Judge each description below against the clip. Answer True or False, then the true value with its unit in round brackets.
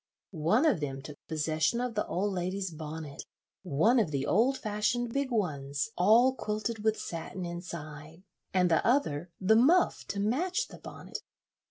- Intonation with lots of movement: True (6.6 semitones)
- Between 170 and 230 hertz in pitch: True (190 Hz)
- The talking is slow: False (160 wpm)